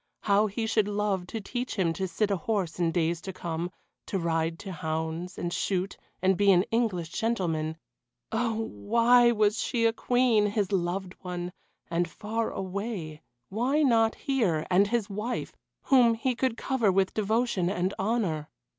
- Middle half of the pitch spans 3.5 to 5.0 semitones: Yes, average, 4.5 semitones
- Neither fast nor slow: Yes, average, 165 wpm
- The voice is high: Yes, high, 200 Hz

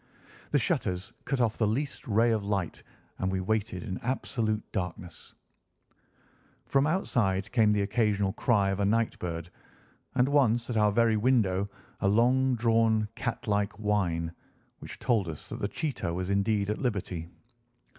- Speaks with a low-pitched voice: Yes, low, 105 Hz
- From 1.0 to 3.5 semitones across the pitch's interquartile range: Yes, average, 3.2 semitones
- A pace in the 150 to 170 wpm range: Yes, average, 155 wpm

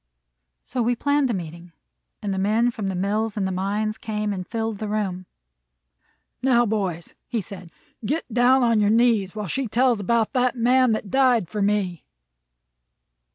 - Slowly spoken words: No, average, 170 wpm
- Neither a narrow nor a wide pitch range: Yes, average, 3.6 semitones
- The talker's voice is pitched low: No, high, 215 Hz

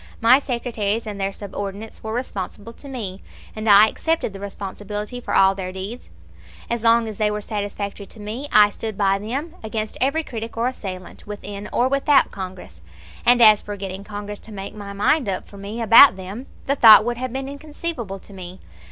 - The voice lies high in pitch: Yes, high, 210 Hz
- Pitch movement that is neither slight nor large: Yes, average, 3.1 semitones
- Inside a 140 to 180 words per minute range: No, average, 195 wpm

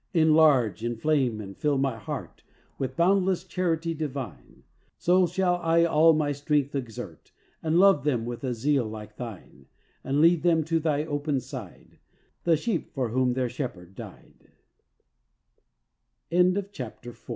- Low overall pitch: No, medium, 145 Hz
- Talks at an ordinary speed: No, slow, 130 wpm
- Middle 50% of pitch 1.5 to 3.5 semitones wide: No, average, 5.0 semitones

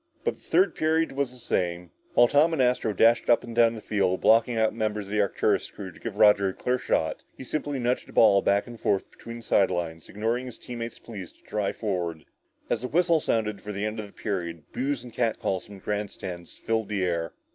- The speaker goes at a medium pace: No, fast, 235 wpm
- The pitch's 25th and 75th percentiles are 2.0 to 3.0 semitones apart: No, average, 3.7 semitones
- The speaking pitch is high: No, low, 110 Hz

